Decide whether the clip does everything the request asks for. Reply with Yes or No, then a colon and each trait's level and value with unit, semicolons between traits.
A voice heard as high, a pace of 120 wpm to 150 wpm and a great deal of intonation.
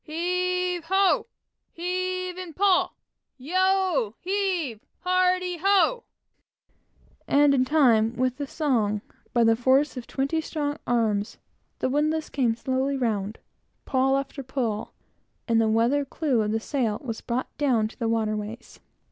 Yes: very high, 275 Hz; slow, 135 wpm; wide, 7.5 semitones